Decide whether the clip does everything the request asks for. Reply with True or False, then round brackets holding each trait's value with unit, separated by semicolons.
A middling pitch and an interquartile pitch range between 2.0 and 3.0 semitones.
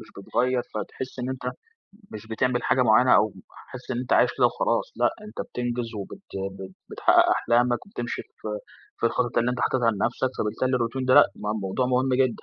False (120 Hz; 2.5 semitones)